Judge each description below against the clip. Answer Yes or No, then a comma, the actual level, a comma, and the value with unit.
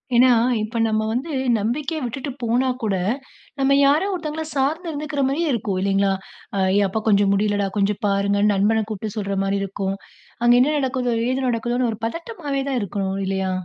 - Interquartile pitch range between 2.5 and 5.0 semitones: No, wide, 5.5 semitones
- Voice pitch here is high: Yes, high, 230 Hz